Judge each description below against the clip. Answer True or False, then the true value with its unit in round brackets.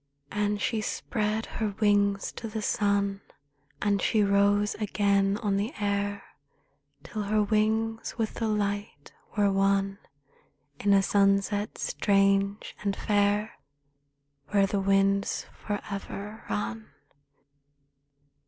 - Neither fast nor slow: False (110 wpm)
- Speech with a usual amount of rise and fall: False (1.0 semitones)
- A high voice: True (205 Hz)